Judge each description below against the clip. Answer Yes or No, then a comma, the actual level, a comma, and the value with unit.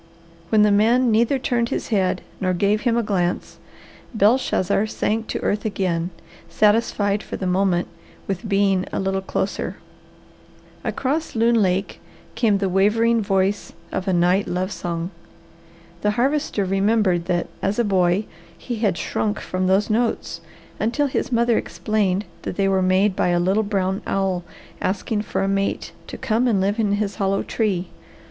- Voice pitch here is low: No, high, 200 Hz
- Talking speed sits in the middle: Yes, average, 160 wpm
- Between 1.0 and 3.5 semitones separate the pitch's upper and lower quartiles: Yes, narrow, 2.6 semitones